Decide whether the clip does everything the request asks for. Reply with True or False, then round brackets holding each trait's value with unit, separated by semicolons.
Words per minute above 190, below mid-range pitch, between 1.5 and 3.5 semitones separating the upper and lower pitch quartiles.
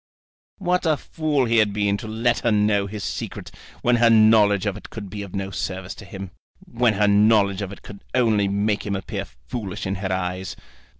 True (205 wpm; 105 Hz; 2.5 semitones)